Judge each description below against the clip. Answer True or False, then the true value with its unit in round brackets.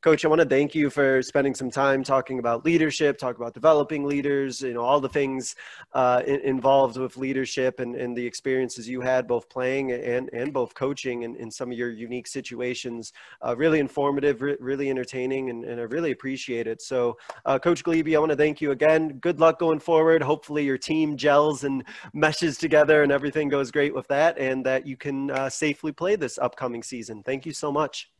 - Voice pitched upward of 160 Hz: False (135 Hz)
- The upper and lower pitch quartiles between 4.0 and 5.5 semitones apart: False (2.7 semitones)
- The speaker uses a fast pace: True (210 wpm)